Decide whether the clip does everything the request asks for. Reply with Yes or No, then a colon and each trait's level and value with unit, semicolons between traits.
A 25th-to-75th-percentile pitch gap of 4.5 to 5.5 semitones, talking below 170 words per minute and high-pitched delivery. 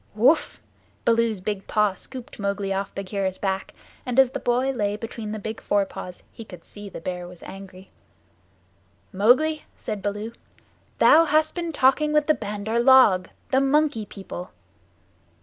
Yes: average, 5.0 semitones; average, 155 wpm; high, 215 Hz